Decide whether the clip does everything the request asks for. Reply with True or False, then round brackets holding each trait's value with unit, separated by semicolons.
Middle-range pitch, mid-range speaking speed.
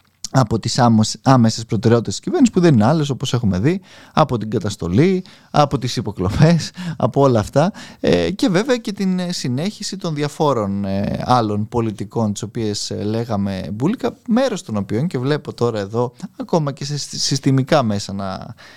False (130 Hz; 155 wpm)